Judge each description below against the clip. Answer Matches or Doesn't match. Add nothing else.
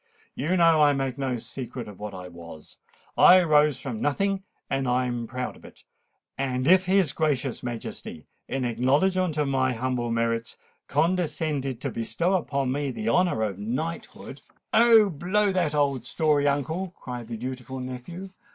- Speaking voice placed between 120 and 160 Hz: Matches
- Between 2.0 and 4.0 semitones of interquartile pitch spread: Doesn't match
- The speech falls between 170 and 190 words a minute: Doesn't match